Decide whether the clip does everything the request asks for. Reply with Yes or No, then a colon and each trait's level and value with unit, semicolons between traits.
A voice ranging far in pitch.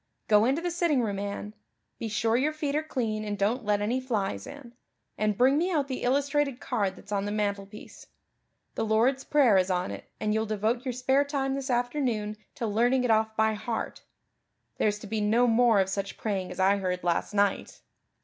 No: average, 4.1 semitones